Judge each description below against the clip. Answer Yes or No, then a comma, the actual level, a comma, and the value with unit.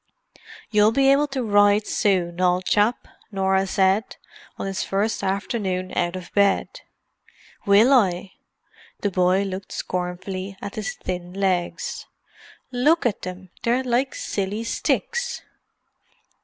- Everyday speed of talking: No, slow, 120 wpm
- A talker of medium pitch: No, high, 200 Hz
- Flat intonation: No, average, 3.4 semitones